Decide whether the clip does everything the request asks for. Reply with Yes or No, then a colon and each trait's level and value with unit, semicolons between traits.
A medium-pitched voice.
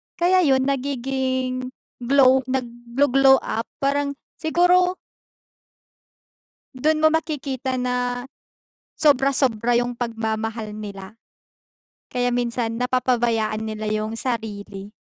No: very high, 250 Hz